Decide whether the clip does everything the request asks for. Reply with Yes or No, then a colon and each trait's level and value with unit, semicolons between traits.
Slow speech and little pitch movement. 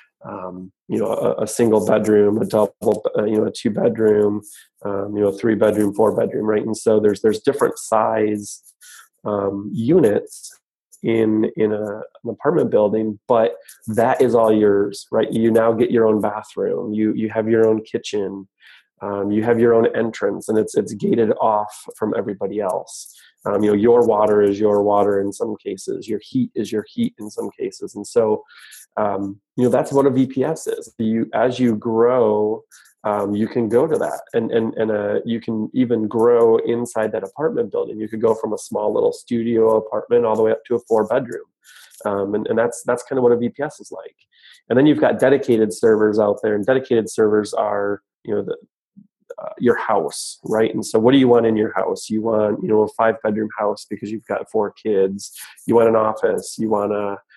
No: fast, 205 wpm; narrow, 2.3 semitones